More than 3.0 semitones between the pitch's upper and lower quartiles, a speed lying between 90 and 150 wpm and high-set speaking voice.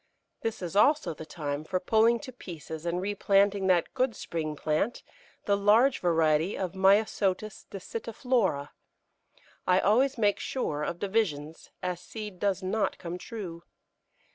Yes: average, 4.4 semitones; average, 140 wpm; high, 195 Hz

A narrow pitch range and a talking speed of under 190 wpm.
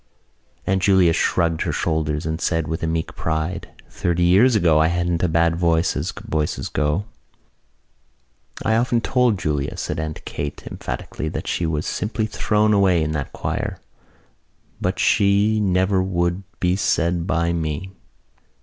No: average, 3.3 semitones; average, 150 wpm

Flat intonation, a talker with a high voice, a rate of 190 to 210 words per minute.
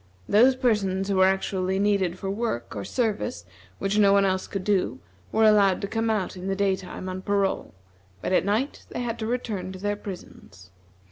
Yes: narrow, 2.1 semitones; high, 195 Hz; average, 200 wpm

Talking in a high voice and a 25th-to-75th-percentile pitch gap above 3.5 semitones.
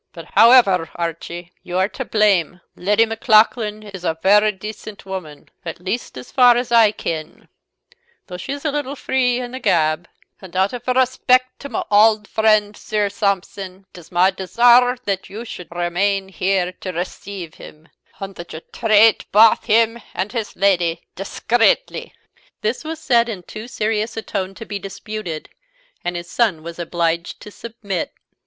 Yes: high, 205 Hz; average, 4.2 semitones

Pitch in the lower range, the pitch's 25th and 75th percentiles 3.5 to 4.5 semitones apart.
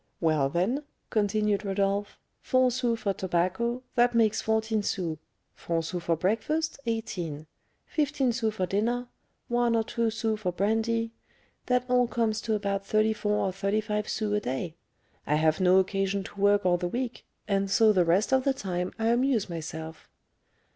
No: high, 210 Hz; average, 3.9 semitones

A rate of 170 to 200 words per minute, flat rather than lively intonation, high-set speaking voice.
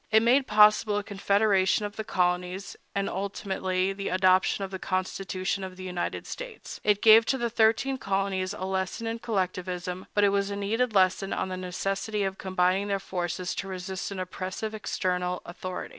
Yes: average, 180 wpm; narrow, 2.0 semitones; high, 195 Hz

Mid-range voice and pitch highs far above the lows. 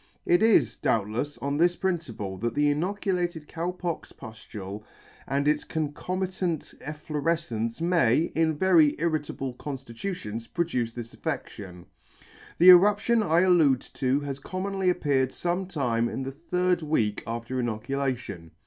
Yes: medium, 150 Hz; wide, 6.5 semitones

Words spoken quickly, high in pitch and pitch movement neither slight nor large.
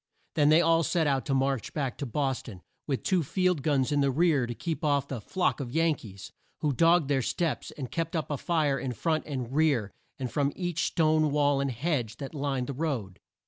No: fast, 225 wpm; medium, 145 Hz; average, 3.3 semitones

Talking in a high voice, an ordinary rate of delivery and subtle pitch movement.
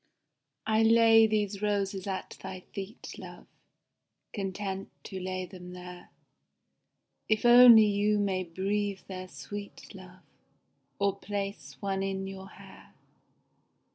No: high, 195 Hz; slow, 115 wpm; narrow, 1.7 semitones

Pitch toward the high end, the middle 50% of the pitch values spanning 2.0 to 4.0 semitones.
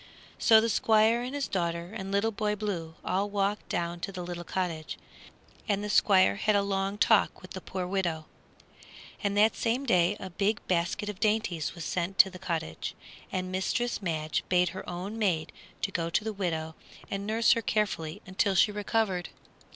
Yes: high, 195 Hz; average, 3.3 semitones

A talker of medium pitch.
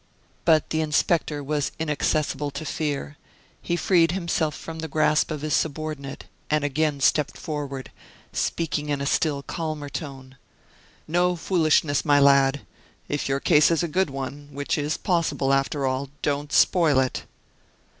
Yes: medium, 150 Hz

